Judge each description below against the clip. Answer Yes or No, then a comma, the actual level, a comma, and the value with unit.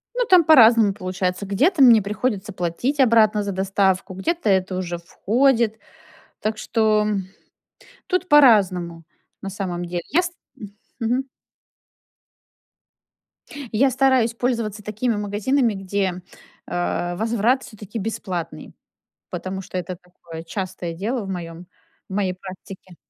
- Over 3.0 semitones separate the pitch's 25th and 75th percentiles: Yes, average, 4.3 semitones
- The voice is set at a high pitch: Yes, high, 205 Hz